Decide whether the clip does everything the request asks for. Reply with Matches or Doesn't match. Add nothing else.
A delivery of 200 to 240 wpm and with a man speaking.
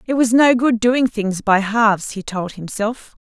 Doesn't match